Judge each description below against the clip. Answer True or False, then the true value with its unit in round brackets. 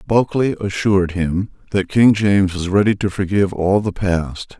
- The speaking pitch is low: True (95 Hz)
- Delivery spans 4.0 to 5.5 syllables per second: True (5.0 syllables/s)